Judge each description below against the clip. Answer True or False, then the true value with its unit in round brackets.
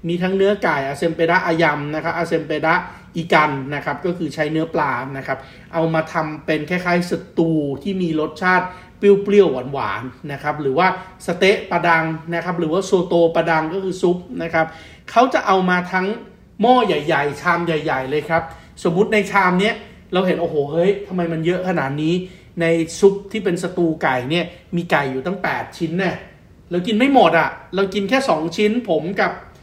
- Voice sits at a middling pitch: True (170 Hz)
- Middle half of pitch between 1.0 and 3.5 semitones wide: True (2.7 semitones)